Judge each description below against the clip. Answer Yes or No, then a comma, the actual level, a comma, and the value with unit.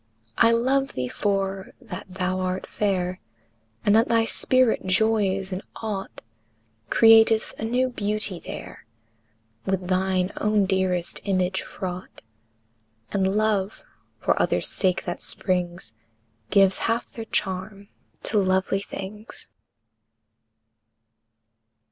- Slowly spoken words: Yes, slow, 110 wpm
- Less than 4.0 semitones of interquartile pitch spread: Yes, narrow, 2.6 semitones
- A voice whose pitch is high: Yes, high, 195 Hz